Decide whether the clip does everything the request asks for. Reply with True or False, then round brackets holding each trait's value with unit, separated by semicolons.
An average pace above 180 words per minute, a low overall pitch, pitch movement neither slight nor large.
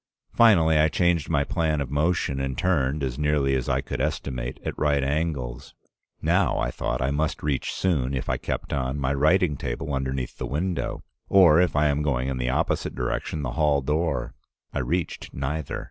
True (190 wpm; 70 Hz; 3.1 semitones)